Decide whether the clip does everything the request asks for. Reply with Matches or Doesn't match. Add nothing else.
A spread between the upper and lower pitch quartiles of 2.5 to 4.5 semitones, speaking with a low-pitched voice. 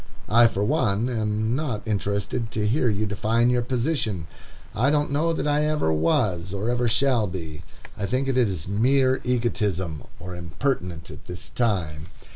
Doesn't match